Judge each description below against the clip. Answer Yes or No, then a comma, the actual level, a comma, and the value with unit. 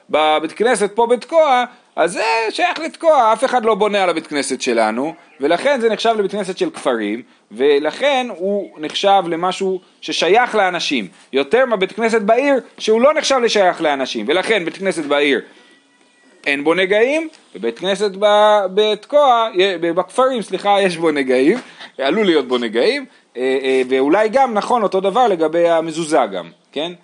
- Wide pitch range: Yes, wide, 6.1 semitones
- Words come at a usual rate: No, fast, 155 wpm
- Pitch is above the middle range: Yes, high, 195 Hz